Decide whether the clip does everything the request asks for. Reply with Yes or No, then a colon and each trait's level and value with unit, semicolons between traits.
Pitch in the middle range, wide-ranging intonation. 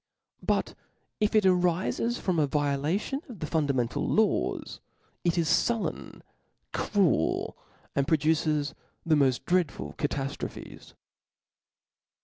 No: medium, 160 Hz; average, 4.6 semitones